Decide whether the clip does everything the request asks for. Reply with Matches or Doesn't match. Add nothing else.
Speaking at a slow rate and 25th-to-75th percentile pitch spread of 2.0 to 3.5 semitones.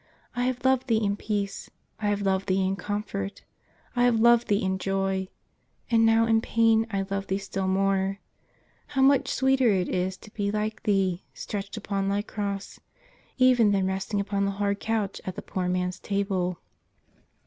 Doesn't match